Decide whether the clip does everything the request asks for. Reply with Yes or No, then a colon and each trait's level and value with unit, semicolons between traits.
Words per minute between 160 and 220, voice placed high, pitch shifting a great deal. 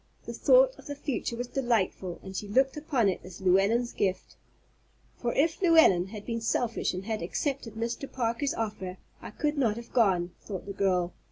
Yes: average, 185 wpm; high, 225 Hz; wide, 5.7 semitones